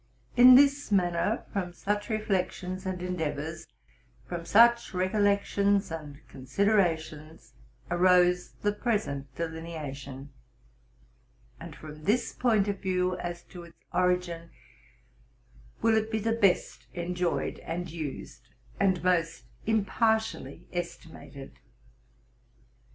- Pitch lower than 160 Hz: No, medium, 180 Hz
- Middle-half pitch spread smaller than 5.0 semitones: Yes, average, 3.6 semitones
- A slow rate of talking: Yes, slow, 105 wpm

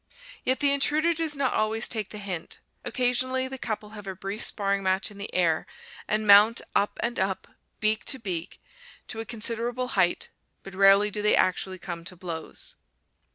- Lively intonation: No, average, 4.0 semitones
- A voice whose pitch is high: Yes, high, 210 Hz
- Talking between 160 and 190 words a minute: Yes, average, 180 wpm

